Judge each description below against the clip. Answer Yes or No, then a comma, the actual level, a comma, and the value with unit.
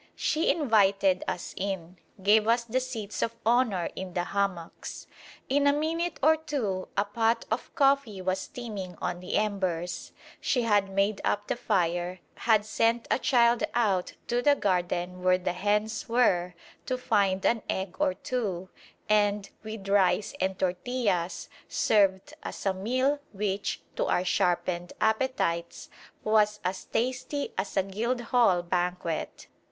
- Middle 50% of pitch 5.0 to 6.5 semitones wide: No, average, 4.2 semitones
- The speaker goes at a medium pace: Yes, average, 145 wpm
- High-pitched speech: Yes, high, 205 Hz